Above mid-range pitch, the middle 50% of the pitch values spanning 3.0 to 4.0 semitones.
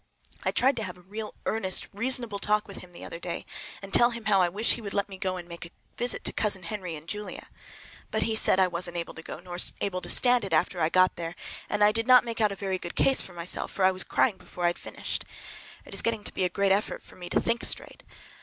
Yes: high, 195 Hz; average, 3.5 semitones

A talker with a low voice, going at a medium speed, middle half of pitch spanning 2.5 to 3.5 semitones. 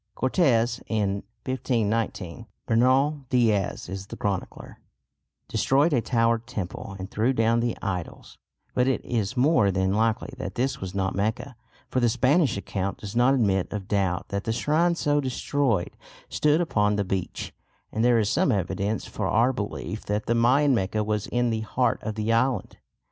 No: low, 115 Hz; average, 170 wpm; average, 4.1 semitones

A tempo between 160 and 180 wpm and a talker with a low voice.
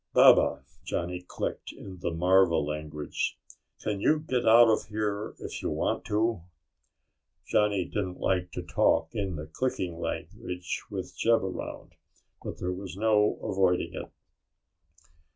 No: slow, 135 wpm; very low, 95 Hz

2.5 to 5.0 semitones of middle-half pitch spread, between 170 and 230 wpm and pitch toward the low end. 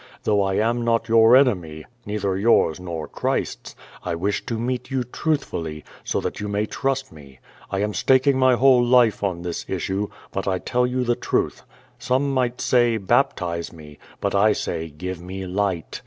No: wide, 5.5 semitones; average, 185 wpm; low, 105 Hz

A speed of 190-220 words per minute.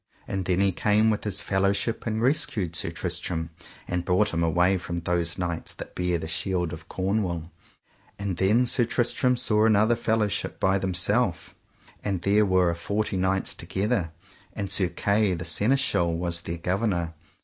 No: average, 165 wpm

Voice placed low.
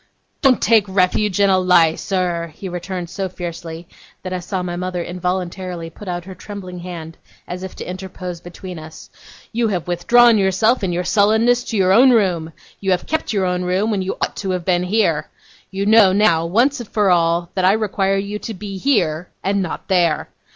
No: medium, 185 Hz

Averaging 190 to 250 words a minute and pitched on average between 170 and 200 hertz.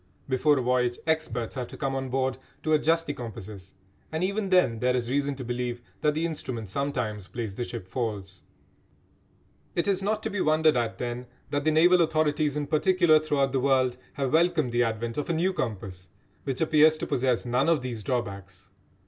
No: average, 195 wpm; low, 135 Hz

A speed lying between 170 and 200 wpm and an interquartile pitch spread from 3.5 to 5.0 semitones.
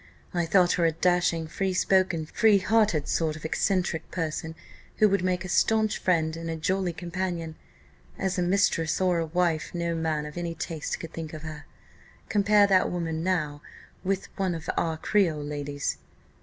No: average, 175 wpm; average, 2.7 semitones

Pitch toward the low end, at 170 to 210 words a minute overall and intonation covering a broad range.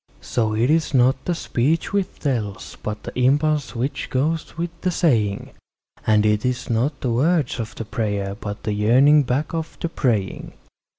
Yes: low, 125 Hz; average, 175 wpm; wide, 5.9 semitones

